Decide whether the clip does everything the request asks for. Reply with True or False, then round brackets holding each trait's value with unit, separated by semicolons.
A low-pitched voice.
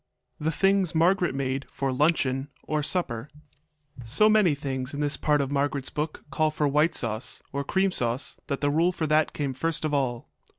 False (145 Hz)